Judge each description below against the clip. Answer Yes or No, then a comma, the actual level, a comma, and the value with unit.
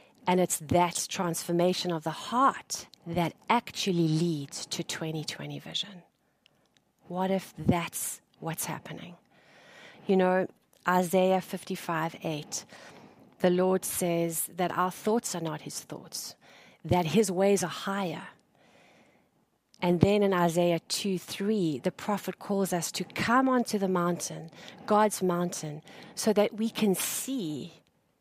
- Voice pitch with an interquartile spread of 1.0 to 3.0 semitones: Yes, average, 2.7 semitones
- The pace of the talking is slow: Yes, slow, 130 wpm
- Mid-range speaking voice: Yes, medium, 180 Hz